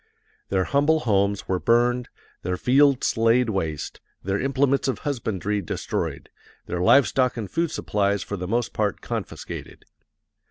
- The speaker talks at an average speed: Yes, average, 145 wpm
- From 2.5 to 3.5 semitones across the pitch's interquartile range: No, average, 5.2 semitones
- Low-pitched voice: Yes, low, 115 Hz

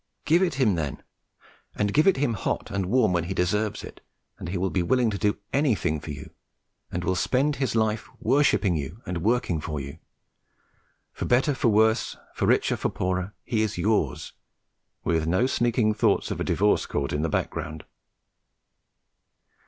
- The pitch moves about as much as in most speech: No, wide, 5.7 semitones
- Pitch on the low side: Yes, low, 105 Hz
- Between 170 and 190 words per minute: Yes, average, 175 wpm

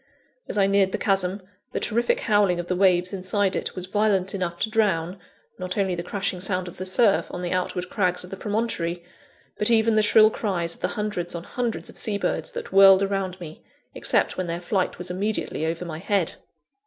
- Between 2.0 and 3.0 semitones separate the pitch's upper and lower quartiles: Yes, narrow, 2.4 semitones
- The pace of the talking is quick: Yes, fast, 210 wpm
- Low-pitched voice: No, high, 190 Hz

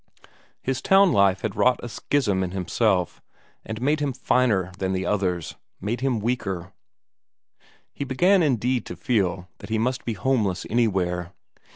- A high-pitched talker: No, low, 110 Hz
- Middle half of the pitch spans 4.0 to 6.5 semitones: Yes, average, 5.3 semitones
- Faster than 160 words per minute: No, average, 155 wpm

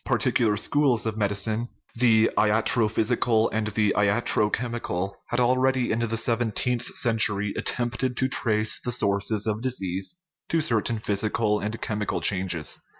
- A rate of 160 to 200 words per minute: No, average, 140 wpm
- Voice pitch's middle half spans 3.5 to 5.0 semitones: No, narrow, 2.4 semitones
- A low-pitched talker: Yes, low, 110 Hz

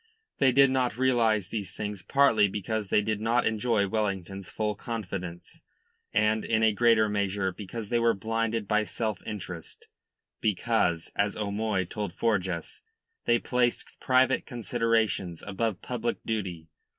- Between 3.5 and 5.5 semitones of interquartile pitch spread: No, average, 2.8 semitones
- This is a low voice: Yes, low, 110 Hz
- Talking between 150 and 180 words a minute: No, average, 140 wpm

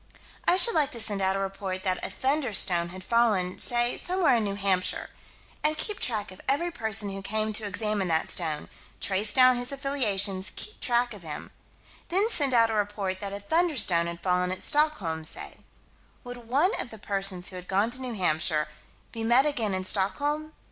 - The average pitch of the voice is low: No, high, 210 Hz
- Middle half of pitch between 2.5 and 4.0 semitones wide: No, average, 5.2 semitones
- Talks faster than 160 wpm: Yes, average, 195 wpm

